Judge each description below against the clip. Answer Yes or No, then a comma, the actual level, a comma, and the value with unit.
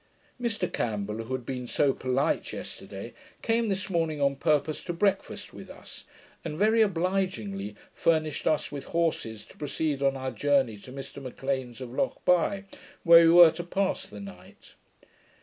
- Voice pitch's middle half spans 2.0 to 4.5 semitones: No, wide, 5.5 semitones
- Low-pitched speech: No, medium, 150 Hz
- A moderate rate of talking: Yes, average, 160 wpm